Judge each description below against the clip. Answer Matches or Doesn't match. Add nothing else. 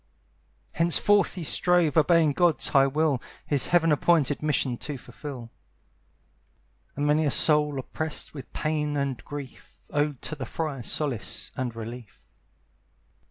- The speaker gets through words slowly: Matches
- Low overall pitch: Doesn't match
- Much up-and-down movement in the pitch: Doesn't match